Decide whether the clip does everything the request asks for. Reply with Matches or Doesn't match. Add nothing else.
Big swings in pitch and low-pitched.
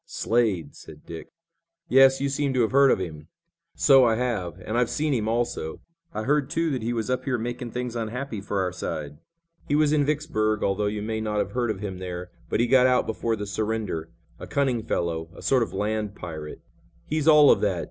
Doesn't match